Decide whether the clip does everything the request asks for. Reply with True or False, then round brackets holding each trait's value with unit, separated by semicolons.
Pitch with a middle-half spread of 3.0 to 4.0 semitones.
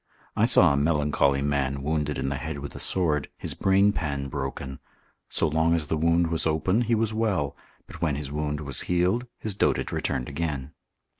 True (3.5 semitones)